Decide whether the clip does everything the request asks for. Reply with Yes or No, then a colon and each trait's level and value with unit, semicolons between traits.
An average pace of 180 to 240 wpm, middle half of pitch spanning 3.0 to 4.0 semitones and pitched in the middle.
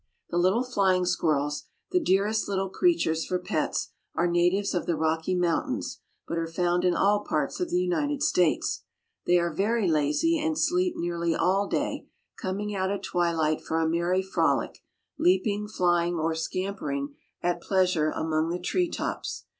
No: average, 160 wpm; average, 3.4 semitones; medium, 180 Hz